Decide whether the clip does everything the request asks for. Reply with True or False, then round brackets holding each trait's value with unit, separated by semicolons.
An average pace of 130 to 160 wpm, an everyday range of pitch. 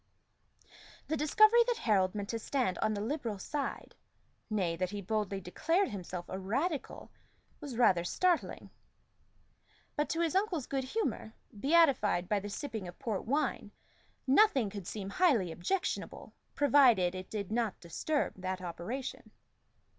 False (140 wpm; 7.5 semitones)